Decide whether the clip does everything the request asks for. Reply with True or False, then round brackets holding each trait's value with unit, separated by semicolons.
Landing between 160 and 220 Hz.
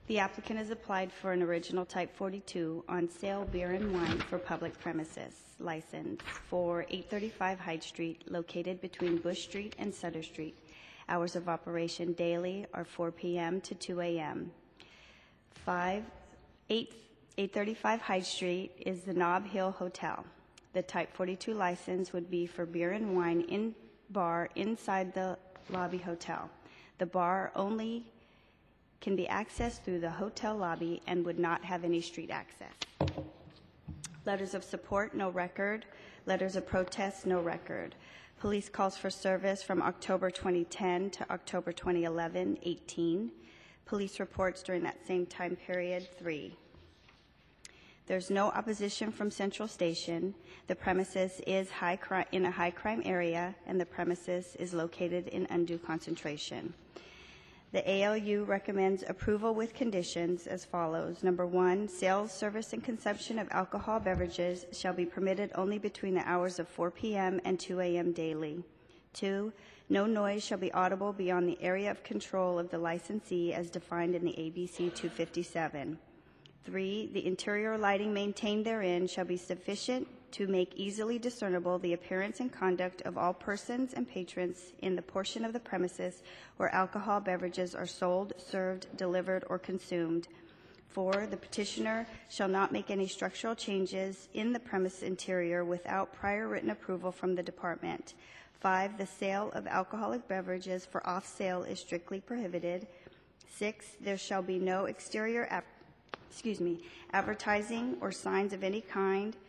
True (185 Hz)